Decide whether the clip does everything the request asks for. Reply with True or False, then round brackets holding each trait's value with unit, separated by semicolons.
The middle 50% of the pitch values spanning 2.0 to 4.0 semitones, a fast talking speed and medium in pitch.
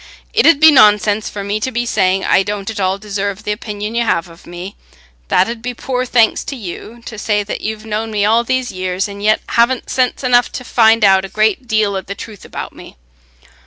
False (2.9 semitones; 230 wpm; 215 Hz)